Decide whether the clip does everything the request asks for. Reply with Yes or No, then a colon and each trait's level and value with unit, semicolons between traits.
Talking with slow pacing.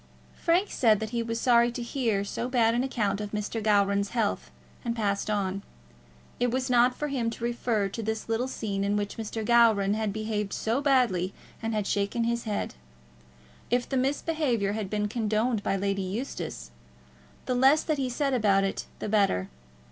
No: average, 185 wpm